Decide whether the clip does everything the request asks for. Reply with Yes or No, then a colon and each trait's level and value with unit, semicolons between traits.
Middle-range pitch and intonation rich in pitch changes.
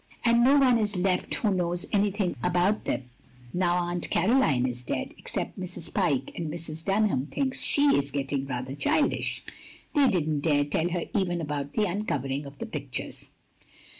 Yes: medium, 175 Hz; wide, 6.2 semitones